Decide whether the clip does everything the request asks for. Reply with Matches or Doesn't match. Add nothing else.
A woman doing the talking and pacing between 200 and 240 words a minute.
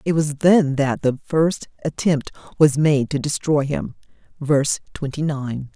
Doesn't match